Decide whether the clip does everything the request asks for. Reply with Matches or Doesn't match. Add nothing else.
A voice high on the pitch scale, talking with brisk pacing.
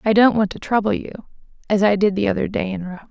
Matches